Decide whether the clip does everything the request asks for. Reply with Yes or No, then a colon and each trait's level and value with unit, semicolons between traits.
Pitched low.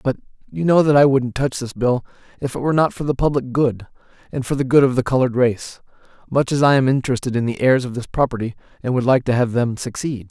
Yes: low, 130 Hz